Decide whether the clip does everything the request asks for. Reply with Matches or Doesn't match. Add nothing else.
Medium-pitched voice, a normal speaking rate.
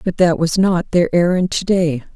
Doesn't match